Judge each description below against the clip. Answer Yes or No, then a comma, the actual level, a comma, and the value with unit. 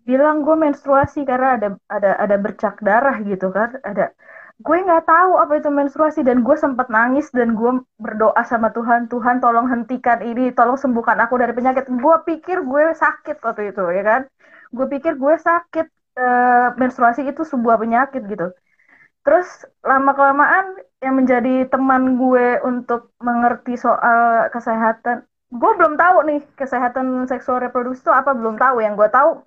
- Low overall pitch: No, very high, 255 Hz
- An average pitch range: Yes, average, 3.5 semitones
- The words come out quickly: Yes, fast, 160 wpm